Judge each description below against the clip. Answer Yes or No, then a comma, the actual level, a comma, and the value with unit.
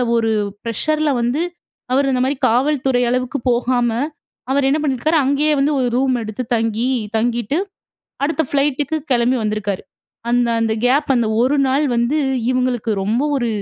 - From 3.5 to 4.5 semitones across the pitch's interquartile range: No, average, 3.0 semitones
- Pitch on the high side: Yes, very high, 255 Hz